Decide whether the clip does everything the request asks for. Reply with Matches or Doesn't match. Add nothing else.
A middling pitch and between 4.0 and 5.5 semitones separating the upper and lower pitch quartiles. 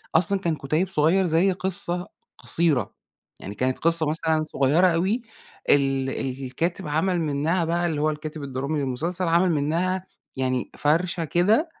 Doesn't match